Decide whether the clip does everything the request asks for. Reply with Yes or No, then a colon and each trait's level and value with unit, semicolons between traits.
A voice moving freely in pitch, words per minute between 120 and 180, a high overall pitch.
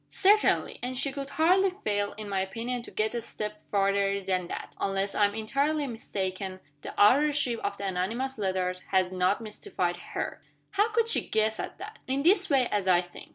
No: wide, 6.1 semitones; average, 195 wpm; high, 215 Hz